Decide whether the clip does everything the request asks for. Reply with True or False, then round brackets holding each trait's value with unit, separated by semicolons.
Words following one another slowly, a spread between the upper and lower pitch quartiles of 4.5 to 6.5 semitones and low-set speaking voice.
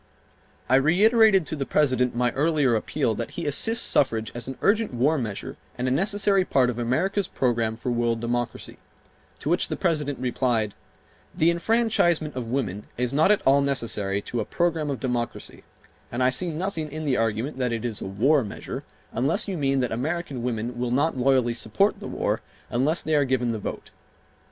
False (190 wpm; 4.9 semitones; 130 Hz)